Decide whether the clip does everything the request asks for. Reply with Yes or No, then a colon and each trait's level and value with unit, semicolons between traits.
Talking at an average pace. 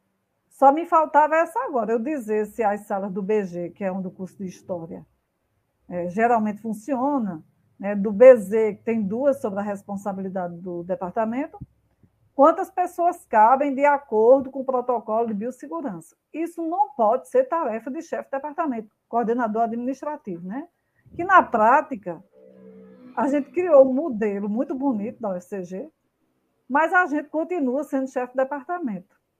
Yes: average, 155 wpm